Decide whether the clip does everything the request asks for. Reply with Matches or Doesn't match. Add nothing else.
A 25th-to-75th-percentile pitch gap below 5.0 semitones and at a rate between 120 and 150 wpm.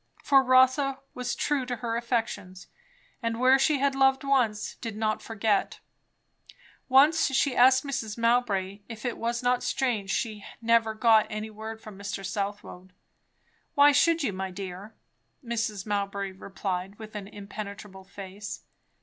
Matches